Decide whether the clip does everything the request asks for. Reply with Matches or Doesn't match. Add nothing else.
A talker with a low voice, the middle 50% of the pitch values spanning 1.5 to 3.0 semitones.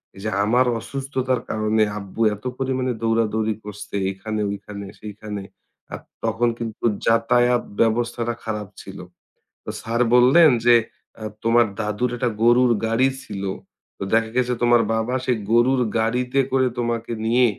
Matches